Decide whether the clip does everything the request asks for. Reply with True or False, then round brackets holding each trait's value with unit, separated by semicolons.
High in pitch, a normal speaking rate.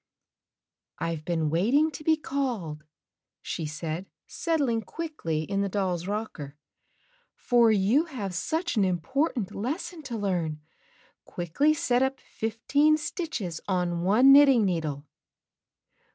False (210 Hz; 125 wpm)